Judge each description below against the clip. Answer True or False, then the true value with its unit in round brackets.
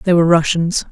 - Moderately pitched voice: True (170 Hz)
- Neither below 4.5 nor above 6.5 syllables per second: True (6.0 syllables/s)